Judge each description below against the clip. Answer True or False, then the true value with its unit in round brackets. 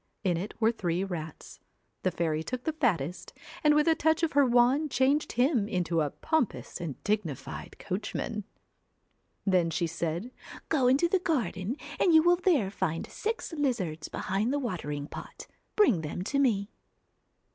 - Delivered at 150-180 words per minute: True (170 wpm)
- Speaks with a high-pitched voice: True (220 Hz)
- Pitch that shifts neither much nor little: False (8.8 semitones)